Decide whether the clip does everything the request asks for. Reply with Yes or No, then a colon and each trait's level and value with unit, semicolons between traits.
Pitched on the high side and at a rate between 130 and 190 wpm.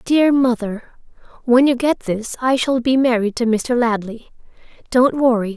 Yes: high, 245 Hz; average, 160 wpm